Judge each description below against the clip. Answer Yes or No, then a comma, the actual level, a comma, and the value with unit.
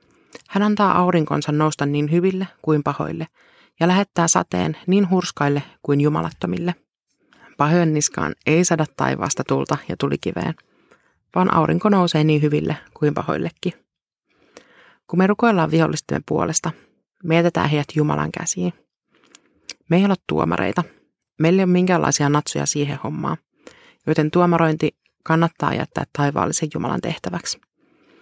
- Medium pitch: Yes, medium, 165 Hz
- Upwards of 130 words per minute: No, average, 120 wpm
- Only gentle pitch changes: No, average, 3.1 semitones